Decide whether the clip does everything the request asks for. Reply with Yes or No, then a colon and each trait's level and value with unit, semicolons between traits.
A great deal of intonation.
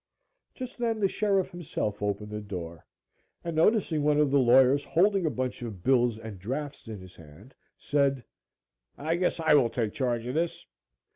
Yes: wide, 6.9 semitones